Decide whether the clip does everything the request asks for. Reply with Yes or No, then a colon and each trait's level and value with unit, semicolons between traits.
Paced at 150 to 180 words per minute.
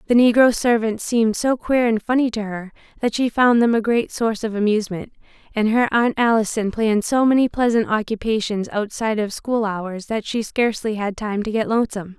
No: average, 195 wpm